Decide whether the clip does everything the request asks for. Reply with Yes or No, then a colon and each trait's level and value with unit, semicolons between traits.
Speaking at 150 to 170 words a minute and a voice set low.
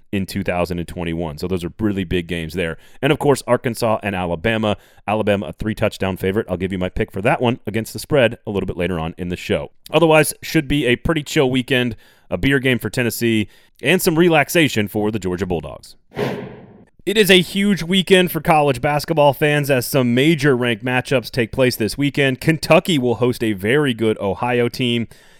No: average, 200 wpm; low, 120 Hz